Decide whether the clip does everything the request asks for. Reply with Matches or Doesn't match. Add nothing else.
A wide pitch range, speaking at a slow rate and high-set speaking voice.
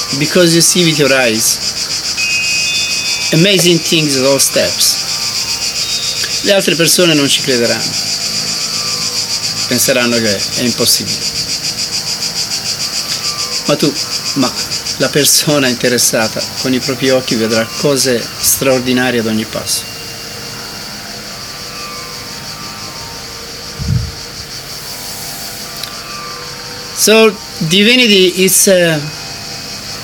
Doesn't match